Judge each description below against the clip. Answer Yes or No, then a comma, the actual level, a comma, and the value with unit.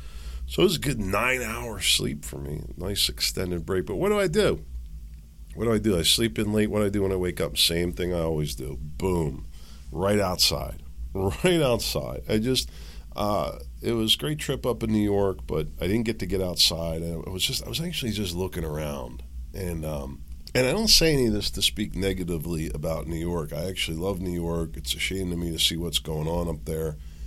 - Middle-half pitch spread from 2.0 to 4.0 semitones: No, wide, 5.5 semitones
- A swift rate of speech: Yes, fast, 225 wpm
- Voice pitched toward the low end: Yes, very low, 85 Hz